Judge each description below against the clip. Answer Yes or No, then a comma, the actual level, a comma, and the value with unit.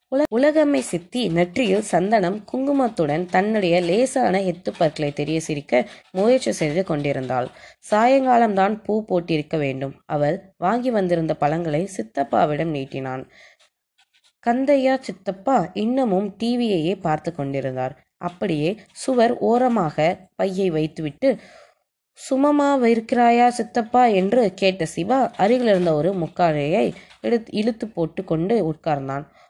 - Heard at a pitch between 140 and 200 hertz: Yes, high, 190 Hz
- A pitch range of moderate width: No, wide, 7.0 semitones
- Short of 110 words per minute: Yes, average, 100 wpm